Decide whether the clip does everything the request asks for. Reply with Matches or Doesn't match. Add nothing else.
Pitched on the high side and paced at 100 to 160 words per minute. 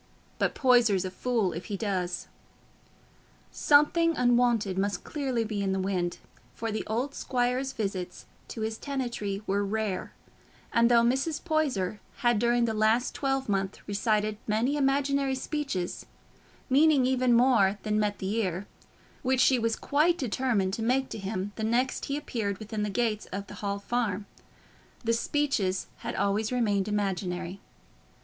Matches